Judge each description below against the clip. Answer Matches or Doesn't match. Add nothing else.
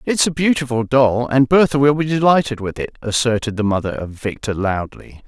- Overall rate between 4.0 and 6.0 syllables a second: Matches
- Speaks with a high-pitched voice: Doesn't match